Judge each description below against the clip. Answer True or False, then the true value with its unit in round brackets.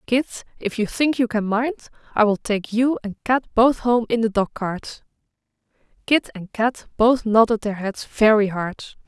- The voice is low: False (225 Hz)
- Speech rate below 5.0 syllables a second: True (4.4 syllables/s)